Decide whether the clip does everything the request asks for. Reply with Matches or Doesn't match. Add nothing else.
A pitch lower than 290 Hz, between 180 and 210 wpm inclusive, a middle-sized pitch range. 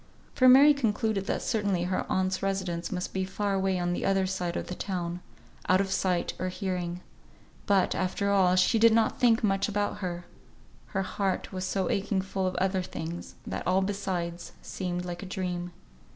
Doesn't match